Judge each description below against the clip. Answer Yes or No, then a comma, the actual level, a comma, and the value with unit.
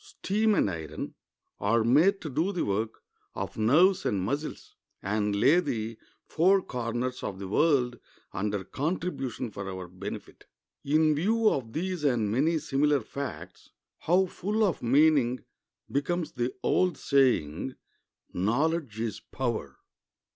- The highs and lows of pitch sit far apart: Yes, wide, 7.1 semitones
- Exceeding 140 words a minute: No, slow, 135 wpm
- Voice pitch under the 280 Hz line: Yes, low, 135 Hz